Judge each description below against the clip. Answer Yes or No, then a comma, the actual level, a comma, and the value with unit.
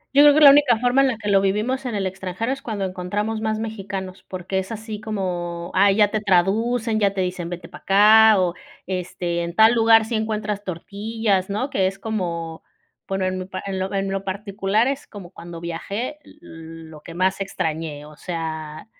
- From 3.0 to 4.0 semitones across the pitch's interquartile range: Yes, average, 3.5 semitones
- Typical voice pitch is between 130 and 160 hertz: No, high, 195 Hz